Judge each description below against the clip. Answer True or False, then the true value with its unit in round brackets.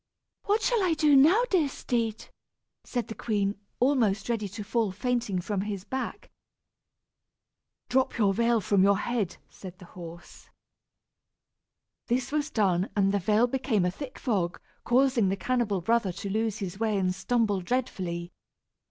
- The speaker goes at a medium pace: True (150 wpm)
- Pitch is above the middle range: True (215 Hz)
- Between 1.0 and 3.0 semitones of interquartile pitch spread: False (4.3 semitones)